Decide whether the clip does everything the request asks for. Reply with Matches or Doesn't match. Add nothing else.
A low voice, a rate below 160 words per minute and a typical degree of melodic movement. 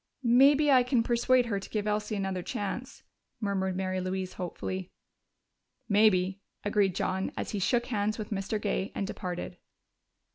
Doesn't match